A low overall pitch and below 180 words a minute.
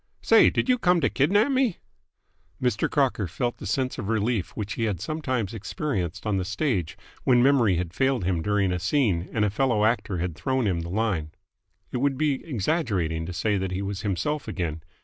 No: low, 110 Hz; average, 200 wpm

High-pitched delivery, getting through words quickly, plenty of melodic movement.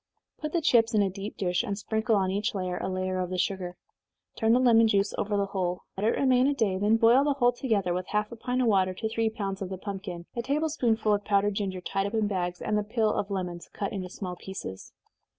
No: high, 205 Hz; fast, 255 wpm; average, 3.3 semitones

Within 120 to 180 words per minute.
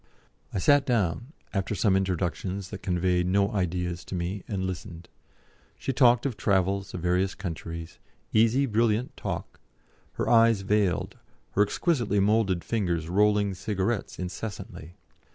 Yes: slow, 135 wpm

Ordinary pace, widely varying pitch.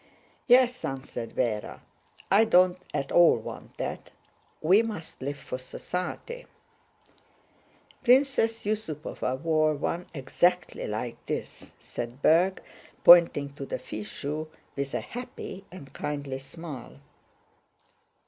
No: slow, 110 wpm; wide, 5.7 semitones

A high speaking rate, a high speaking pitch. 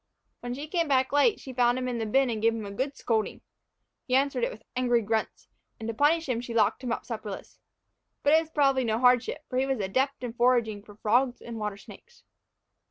Yes: fast, 230 wpm; high, 245 Hz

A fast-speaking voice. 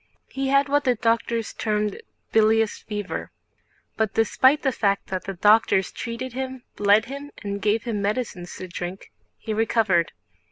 No: average, 155 wpm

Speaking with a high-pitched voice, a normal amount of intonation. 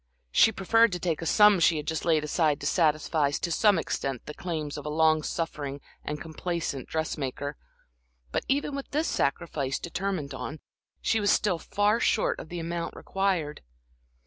No: medium, 165 Hz; average, 4.3 semitones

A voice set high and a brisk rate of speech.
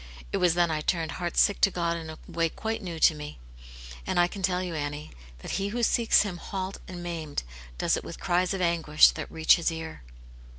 No: medium, 175 Hz; fast, 225 wpm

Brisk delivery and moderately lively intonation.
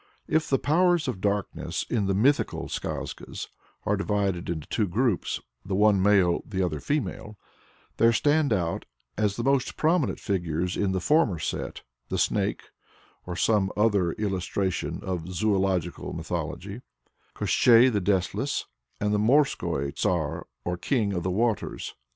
No: average, 145 wpm; average, 4.2 semitones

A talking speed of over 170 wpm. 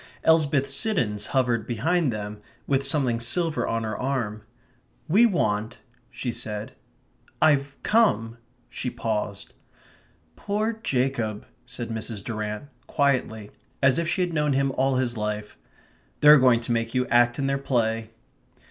No: average, 140 wpm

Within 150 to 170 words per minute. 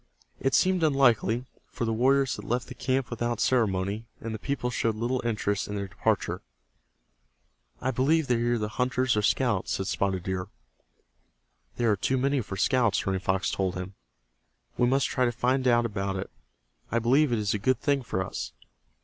No: average, 185 wpm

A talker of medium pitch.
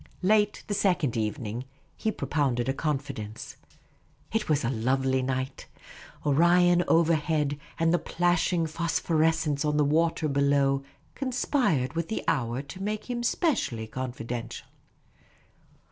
Yes: medium, 150 Hz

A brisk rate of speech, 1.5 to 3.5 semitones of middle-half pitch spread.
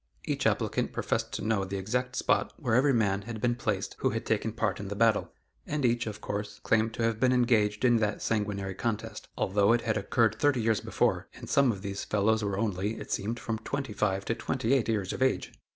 Yes: fast, 225 wpm; average, 2.7 semitones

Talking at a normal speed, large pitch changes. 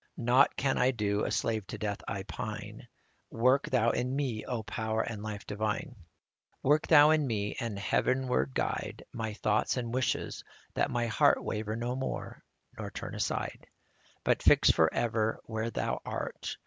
No: average, 165 wpm; average, 2.9 semitones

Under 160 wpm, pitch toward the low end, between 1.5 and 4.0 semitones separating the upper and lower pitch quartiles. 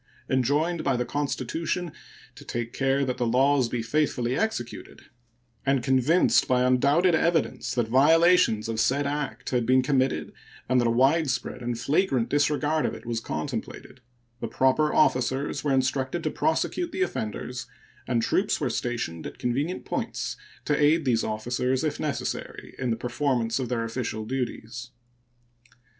Yes: average, 150 wpm; low, 130 Hz; average, 3.4 semitones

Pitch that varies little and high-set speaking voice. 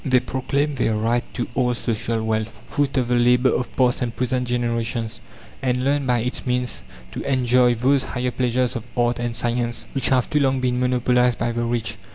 No: narrow, 1.3 semitones; low, 125 Hz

